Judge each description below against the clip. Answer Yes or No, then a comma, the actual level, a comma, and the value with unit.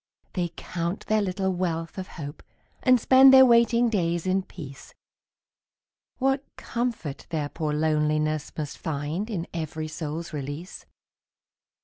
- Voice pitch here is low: No, medium, 170 Hz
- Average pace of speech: No, slow, 125 wpm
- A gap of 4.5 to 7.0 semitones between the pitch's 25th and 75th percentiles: Yes, wide, 5.6 semitones